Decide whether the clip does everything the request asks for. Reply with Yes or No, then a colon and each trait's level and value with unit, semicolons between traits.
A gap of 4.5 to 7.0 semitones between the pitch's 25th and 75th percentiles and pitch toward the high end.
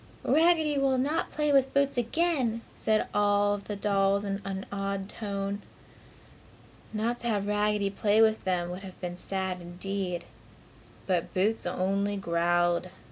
No: average, 2.9 semitones; high, 200 Hz